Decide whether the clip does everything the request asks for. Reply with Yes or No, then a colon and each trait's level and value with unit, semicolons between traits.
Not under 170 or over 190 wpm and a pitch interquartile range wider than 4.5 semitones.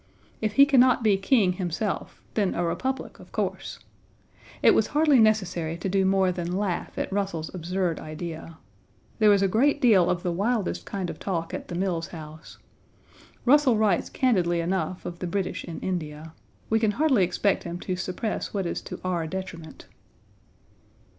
No: average, 175 wpm; average, 3.9 semitones